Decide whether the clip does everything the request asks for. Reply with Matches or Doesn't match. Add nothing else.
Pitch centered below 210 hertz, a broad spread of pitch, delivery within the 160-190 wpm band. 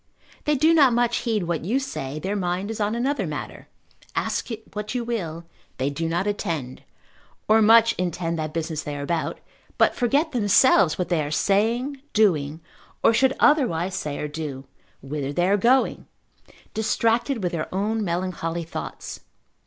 Matches